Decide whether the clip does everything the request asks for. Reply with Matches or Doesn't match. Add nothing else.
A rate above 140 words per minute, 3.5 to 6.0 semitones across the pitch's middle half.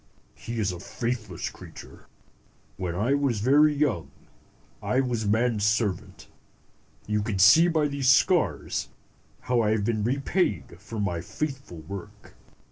Doesn't match